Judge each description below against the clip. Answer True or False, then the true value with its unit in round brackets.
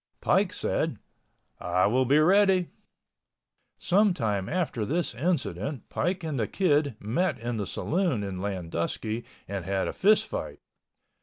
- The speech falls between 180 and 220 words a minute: False (140 wpm)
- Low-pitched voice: True (130 Hz)